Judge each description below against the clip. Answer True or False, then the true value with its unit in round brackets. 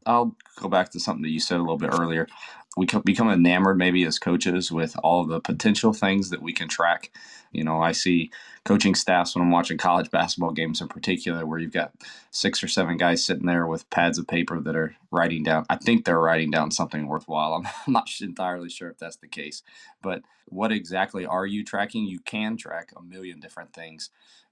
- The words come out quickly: True (210 wpm)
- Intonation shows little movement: True (2.3 semitones)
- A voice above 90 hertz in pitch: False (85 Hz)